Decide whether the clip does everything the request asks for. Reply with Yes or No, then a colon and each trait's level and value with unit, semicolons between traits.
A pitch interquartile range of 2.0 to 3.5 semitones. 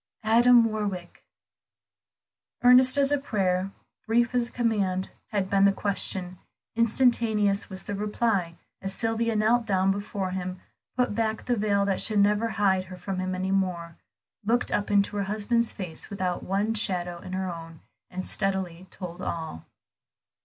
Yes: average, 3.2 semitones